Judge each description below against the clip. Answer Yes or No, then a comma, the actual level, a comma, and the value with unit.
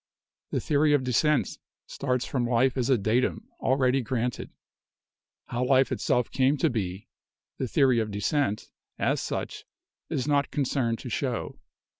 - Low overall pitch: Yes, low, 130 Hz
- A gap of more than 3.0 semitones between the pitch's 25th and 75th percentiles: No, average, 2.7 semitones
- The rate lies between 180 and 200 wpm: No, average, 145 wpm